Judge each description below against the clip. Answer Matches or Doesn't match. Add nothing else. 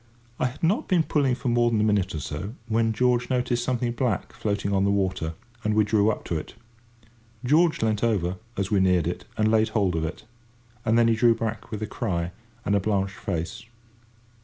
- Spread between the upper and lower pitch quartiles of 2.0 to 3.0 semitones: Doesn't match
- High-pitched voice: Doesn't match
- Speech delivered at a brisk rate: Matches